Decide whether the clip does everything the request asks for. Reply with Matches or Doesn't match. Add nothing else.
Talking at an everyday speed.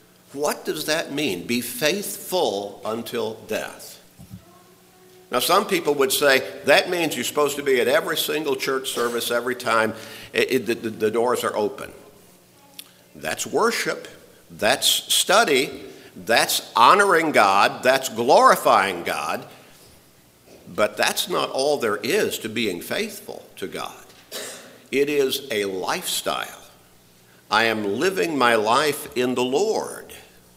Doesn't match